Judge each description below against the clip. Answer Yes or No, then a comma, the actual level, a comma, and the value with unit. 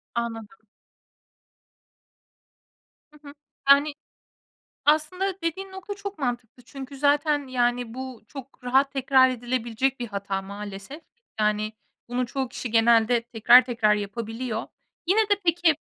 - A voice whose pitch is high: Yes, very high, 255 Hz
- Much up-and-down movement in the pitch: No, average, 4.2 semitones